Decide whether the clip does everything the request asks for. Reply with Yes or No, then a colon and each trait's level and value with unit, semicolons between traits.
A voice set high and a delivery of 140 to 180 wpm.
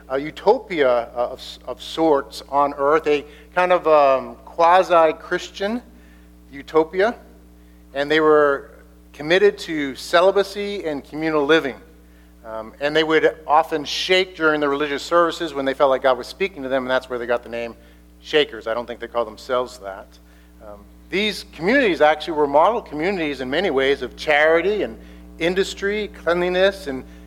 No: medium, 140 Hz; average, 160 wpm